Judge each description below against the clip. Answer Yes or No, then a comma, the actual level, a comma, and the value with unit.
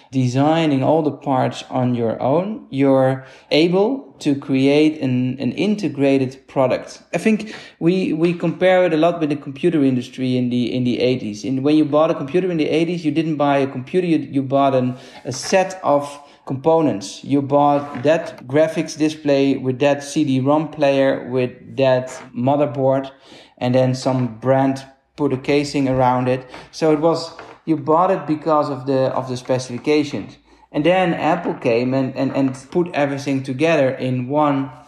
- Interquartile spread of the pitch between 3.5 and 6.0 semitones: No, average, 3.1 semitones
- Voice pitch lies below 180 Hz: Yes, medium, 140 Hz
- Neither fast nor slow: Yes, average, 170 wpm